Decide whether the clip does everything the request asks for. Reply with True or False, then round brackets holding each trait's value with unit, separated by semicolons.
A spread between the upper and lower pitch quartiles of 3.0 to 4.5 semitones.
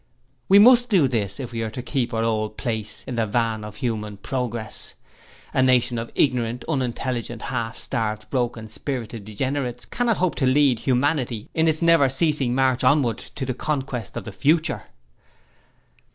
True (3.5 semitones)